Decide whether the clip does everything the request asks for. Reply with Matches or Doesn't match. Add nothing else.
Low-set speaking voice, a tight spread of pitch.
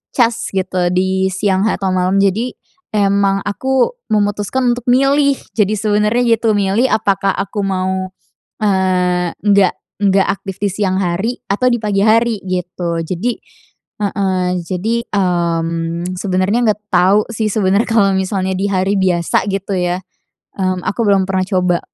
Doesn't match